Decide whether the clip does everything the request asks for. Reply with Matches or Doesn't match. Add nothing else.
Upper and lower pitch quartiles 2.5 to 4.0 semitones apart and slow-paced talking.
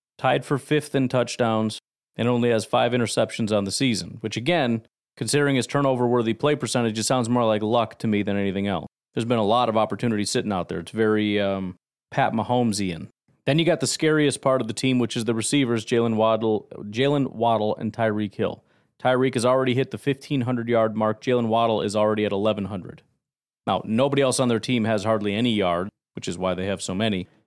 Doesn't match